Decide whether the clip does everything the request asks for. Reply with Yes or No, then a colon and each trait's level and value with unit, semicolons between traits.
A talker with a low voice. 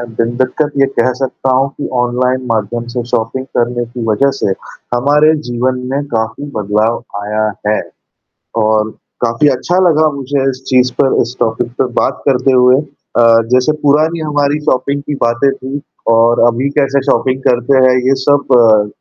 Yes: low, 130 Hz